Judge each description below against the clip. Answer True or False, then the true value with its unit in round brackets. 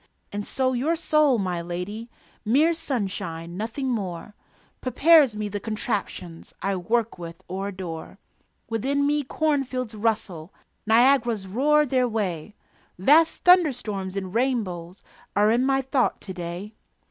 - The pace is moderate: False (130 wpm)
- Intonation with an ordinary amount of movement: False (6.0 semitones)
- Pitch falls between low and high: False (220 Hz)